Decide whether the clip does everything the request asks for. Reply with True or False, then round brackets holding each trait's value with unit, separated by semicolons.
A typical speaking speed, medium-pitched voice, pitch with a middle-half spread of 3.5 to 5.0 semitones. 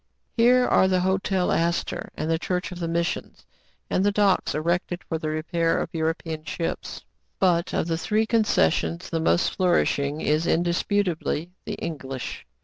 False (165 wpm; 170 Hz; 2.7 semitones)